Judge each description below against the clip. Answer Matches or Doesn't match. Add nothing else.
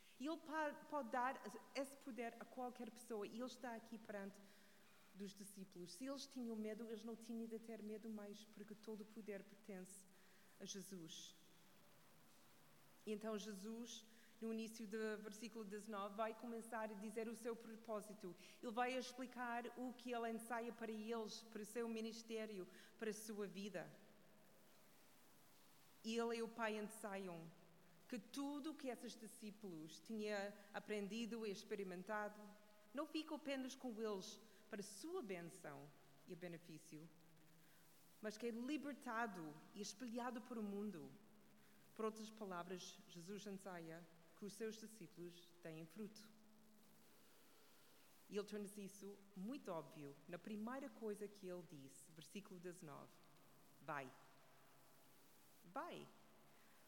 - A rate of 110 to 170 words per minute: Matches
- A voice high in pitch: Matches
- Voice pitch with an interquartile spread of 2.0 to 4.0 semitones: Matches